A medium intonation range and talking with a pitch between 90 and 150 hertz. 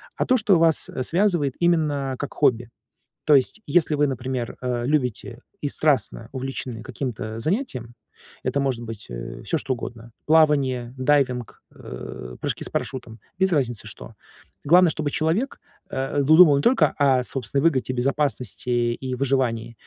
Yes: average, 3.8 semitones; low, 135 Hz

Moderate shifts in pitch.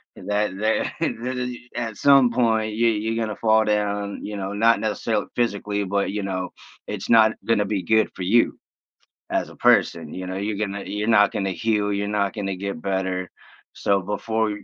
No: narrow, 2.0 semitones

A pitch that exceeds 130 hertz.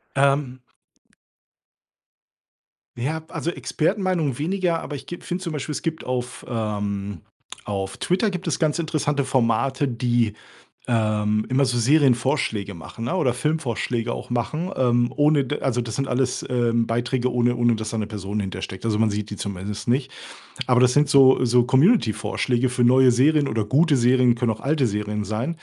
No: low, 125 Hz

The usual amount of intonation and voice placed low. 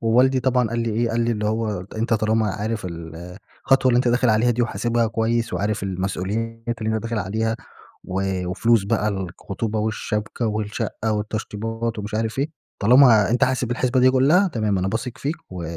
No: narrow, 2.2 semitones; low, 110 Hz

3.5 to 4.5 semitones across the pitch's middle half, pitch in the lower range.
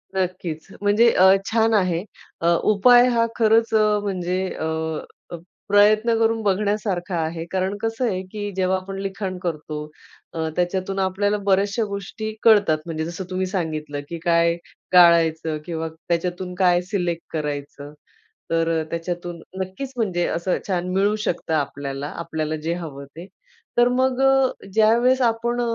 No: average, 3.8 semitones; medium, 185 Hz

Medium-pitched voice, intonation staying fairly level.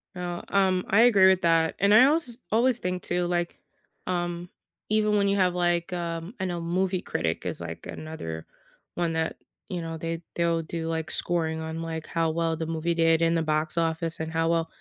Yes: medium, 170 Hz; narrow, 2.0 semitones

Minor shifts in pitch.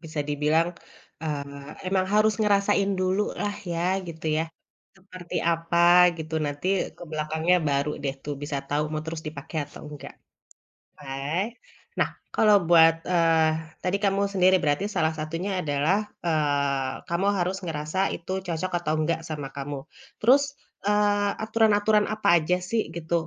No: average, 4.1 semitones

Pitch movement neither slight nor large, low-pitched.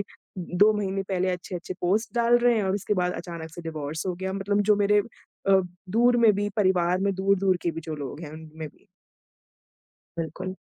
No: average, 3.2 semitones; high, 190 Hz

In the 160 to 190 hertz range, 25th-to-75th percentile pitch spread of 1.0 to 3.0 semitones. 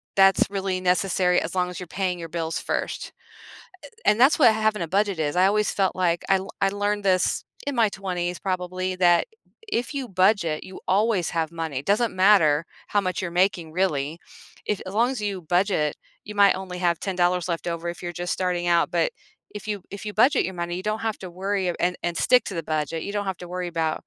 Yes: medium, 185 Hz; average, 2.7 semitones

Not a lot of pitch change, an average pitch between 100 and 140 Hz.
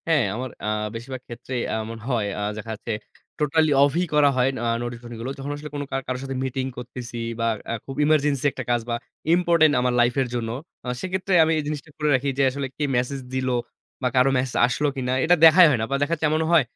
No: average, 3.5 semitones; low, 135 Hz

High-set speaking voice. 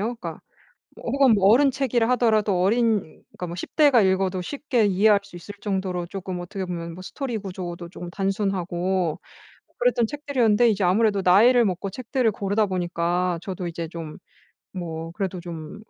Yes: high, 195 Hz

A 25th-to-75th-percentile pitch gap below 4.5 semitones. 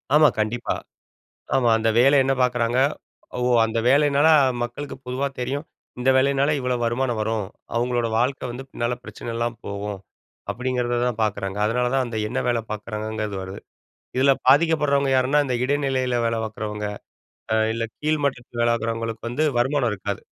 Yes: average, 3.0 semitones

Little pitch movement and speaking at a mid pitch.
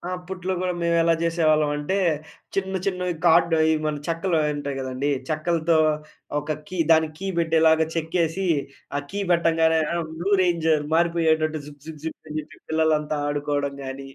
Yes: narrow, 1.9 semitones; medium, 160 Hz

